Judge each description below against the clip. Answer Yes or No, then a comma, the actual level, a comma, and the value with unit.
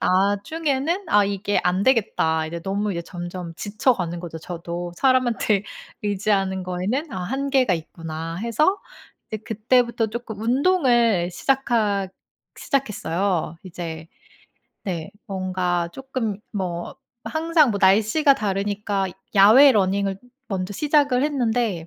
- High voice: Yes, high, 205 Hz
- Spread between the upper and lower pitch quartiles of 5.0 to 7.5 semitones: Yes, wide, 5.5 semitones